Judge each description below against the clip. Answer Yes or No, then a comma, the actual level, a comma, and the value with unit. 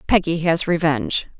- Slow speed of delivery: Yes, slow, 130 wpm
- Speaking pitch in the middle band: Yes, medium, 165 Hz